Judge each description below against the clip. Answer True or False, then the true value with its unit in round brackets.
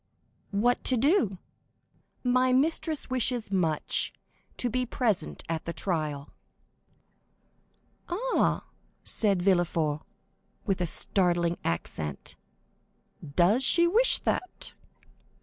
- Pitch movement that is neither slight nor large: False (7.0 semitones)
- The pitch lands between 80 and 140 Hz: False (200 Hz)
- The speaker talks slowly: True (95 wpm)